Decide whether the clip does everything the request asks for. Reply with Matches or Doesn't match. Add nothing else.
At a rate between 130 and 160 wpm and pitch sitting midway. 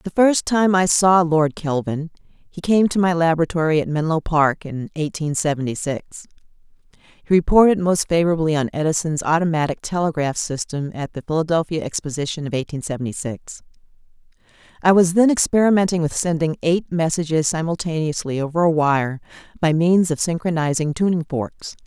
Matches